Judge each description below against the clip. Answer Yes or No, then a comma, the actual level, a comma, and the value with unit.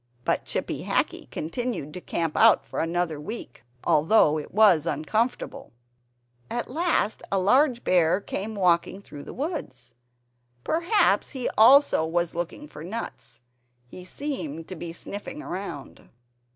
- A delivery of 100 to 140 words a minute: Yes, slow, 135 wpm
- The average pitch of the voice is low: No, medium, 185 Hz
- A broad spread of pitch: Yes, wide, 6.6 semitones